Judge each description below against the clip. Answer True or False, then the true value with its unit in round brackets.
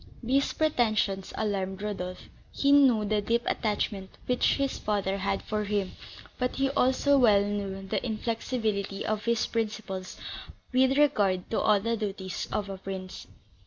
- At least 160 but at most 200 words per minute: False (150 wpm)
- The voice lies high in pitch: True (210 Hz)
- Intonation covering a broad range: False (3.5 semitones)